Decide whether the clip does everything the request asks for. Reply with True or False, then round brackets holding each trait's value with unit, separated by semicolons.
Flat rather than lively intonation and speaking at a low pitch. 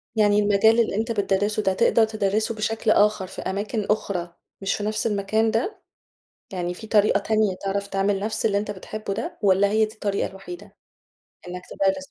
False (1.9 semitones; 210 Hz)